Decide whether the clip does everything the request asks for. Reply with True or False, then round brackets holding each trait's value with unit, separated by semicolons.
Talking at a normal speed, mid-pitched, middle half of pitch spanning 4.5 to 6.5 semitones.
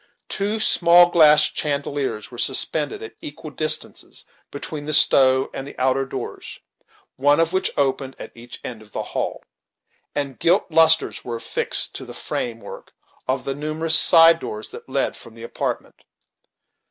False (155 wpm; 145 Hz; 3.7 semitones)